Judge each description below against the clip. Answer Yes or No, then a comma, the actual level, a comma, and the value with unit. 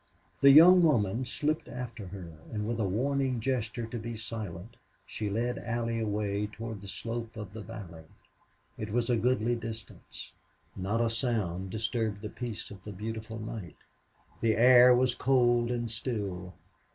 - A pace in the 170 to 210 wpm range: No, average, 160 wpm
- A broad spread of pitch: No, narrow, 2.6 semitones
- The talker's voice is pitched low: Yes, low, 115 Hz